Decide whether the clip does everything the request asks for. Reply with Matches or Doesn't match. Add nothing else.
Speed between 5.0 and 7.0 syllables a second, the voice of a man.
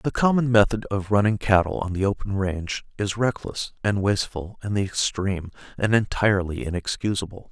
Matches